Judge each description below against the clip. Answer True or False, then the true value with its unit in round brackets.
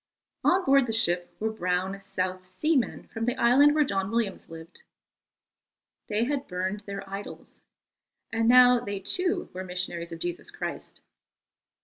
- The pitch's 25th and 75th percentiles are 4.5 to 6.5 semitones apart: True (5.1 semitones)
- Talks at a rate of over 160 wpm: False (150 wpm)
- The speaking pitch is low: False (200 Hz)